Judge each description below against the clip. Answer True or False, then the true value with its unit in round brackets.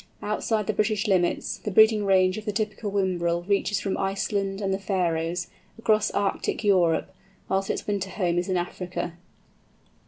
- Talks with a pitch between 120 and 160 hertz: False (195 Hz)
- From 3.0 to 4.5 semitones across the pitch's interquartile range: False (2.5 semitones)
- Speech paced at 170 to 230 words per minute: False (160 wpm)